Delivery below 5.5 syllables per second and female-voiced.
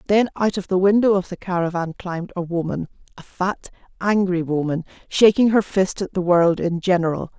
Yes: 5.3 syllables/s; female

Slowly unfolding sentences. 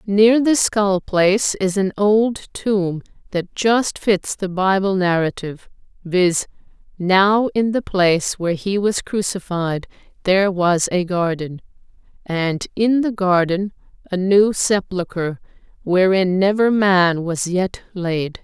Yes: slow, 130 wpm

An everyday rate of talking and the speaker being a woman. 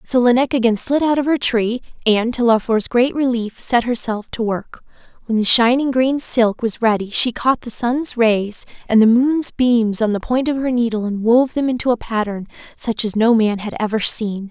No: fast, 215 wpm; female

